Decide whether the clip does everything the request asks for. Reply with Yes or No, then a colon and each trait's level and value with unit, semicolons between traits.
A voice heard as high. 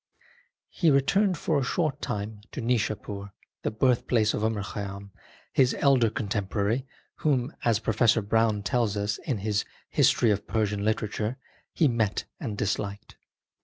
No: low, 110 Hz